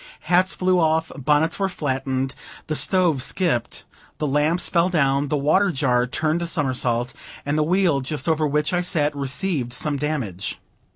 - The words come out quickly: No, average, 165 wpm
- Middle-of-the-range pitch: Yes, medium, 150 Hz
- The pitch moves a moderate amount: Yes, average, 4.0 semitones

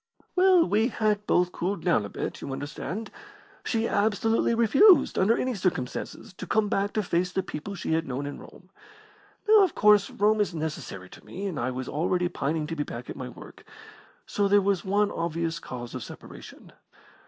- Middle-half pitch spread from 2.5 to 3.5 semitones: No, wide, 5.6 semitones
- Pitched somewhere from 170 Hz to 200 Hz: Yes, high, 190 Hz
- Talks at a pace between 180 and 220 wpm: Yes, average, 190 wpm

